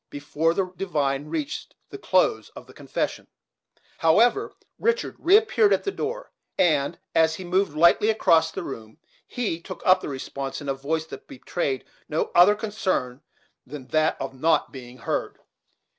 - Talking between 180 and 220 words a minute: No, average, 160 wpm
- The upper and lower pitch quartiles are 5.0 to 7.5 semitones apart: Yes, wide, 5.6 semitones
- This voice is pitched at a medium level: Yes, medium, 160 Hz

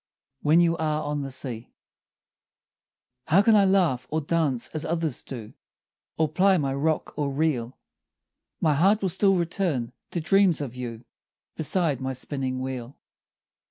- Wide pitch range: No, average, 4.5 semitones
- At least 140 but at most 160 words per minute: Yes, average, 150 wpm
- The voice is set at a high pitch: No, medium, 150 Hz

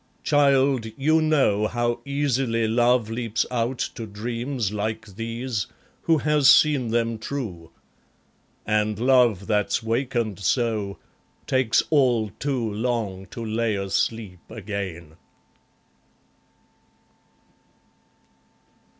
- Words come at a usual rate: No, slow, 95 wpm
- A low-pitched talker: Yes, low, 115 Hz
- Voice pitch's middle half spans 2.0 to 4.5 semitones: Yes, average, 3.5 semitones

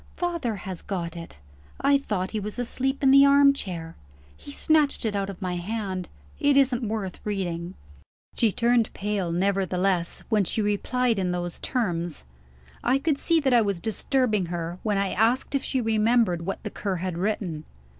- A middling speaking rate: Yes, average, 175 wpm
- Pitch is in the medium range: No, high, 210 Hz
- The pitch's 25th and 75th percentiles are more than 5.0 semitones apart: Yes, wide, 5.4 semitones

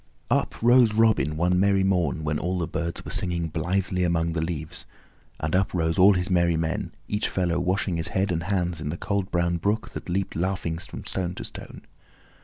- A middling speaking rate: No, fast, 210 wpm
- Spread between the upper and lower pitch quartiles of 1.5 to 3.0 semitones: Yes, narrow, 2.5 semitones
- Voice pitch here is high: No, very low, 90 Hz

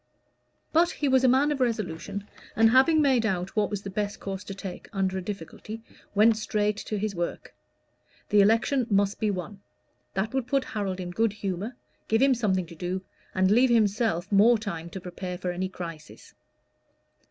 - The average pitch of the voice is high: Yes, high, 205 Hz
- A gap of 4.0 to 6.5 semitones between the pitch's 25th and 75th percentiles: No, average, 3.4 semitones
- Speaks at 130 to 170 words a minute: No, average, 185 wpm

